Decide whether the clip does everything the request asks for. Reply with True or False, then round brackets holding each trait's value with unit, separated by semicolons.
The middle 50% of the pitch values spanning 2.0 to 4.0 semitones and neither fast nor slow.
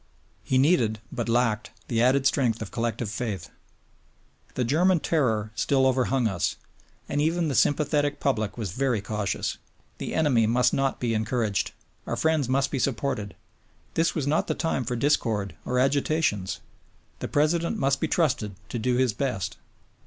False (4.5 semitones; 160 wpm)